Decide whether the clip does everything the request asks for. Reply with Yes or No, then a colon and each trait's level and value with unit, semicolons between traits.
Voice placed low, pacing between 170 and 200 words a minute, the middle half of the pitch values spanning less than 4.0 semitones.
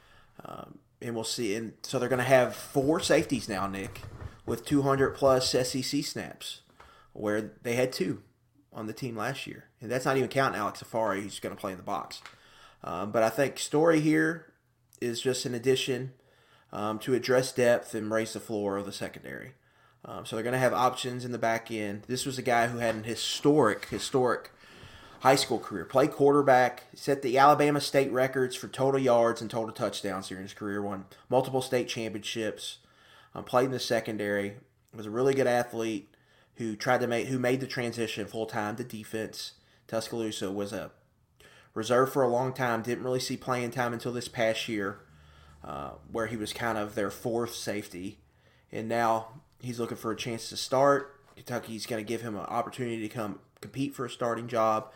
Yes: low, 115 Hz; average, 190 wpm; average, 3.0 semitones